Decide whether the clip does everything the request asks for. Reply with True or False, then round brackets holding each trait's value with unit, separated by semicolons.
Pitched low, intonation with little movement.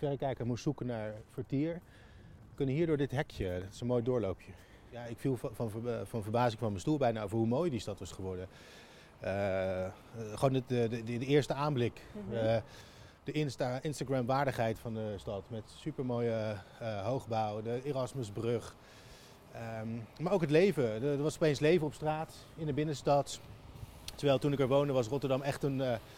False (120 Hz; 4.3 semitones)